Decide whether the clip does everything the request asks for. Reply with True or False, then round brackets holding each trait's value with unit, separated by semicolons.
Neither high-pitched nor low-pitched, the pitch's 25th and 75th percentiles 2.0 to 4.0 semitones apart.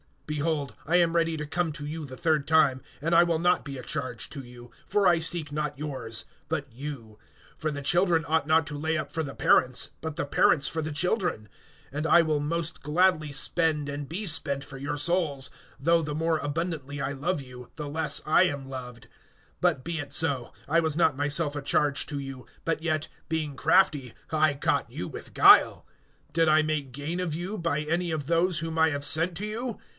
True (155 Hz; 2.6 semitones)